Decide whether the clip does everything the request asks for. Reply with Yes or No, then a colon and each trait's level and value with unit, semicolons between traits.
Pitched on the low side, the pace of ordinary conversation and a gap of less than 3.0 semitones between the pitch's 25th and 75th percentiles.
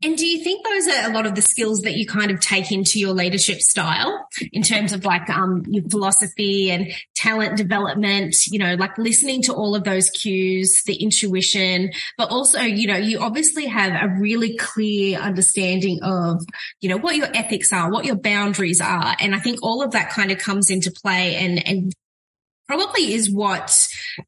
No: high, 200 Hz; average, 195 wpm; narrow, 2.6 semitones